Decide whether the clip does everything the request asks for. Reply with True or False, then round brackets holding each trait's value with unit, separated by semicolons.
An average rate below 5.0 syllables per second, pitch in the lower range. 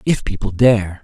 True (4.4 syllables/s; 105 Hz)